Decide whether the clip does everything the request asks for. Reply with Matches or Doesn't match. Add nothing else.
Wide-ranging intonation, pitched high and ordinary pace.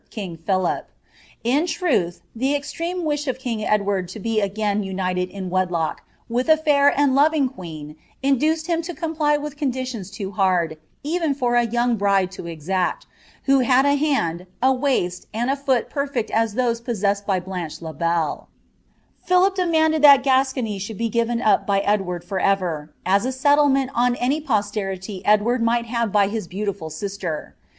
Matches